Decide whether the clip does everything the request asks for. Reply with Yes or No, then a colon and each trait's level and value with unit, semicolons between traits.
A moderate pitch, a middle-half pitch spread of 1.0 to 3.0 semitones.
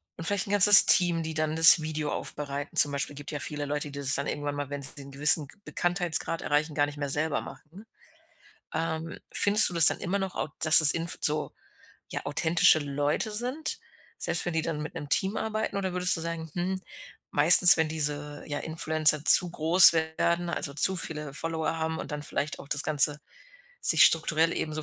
Yes: medium, 160 Hz; average, 2.7 semitones